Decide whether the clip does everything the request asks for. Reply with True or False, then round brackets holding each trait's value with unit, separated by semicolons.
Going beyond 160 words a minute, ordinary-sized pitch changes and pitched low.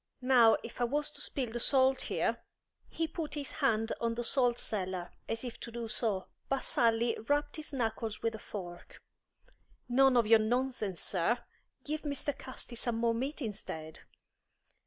False (175 wpm; 3.2 semitones; 235 Hz)